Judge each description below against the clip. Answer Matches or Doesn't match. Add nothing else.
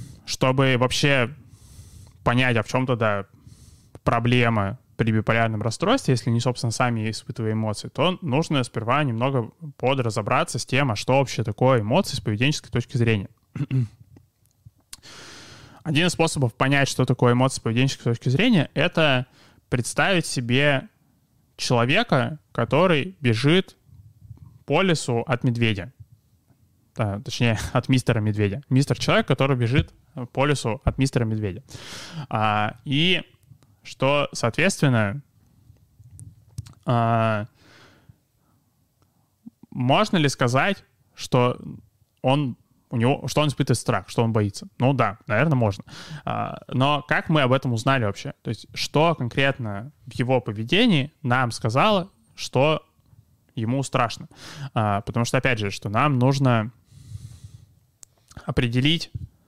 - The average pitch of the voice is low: Matches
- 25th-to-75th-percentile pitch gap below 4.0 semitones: Matches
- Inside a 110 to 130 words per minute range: Matches